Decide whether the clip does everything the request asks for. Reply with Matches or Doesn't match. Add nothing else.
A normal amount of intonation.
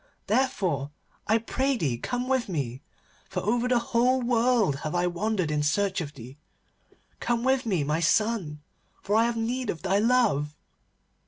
Doesn't match